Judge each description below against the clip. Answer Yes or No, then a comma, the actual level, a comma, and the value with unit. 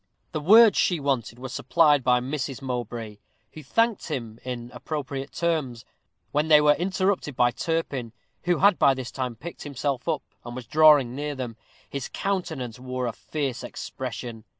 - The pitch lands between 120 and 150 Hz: Yes, low, 135 Hz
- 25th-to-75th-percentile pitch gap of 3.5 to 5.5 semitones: Yes, average, 4.0 semitones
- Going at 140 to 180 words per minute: Yes, average, 165 wpm